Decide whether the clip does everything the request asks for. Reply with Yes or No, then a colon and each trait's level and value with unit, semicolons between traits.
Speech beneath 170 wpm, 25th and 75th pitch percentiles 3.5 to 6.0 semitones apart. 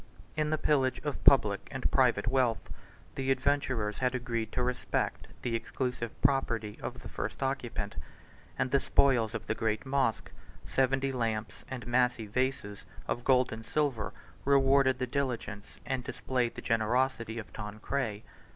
No: average, 150 wpm; average, 2.9 semitones